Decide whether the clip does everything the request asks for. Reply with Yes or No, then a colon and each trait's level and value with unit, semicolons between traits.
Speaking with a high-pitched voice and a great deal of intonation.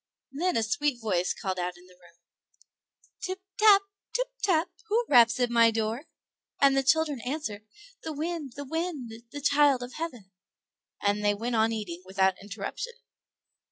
Yes: high, 245 Hz; wide, 7.0 semitones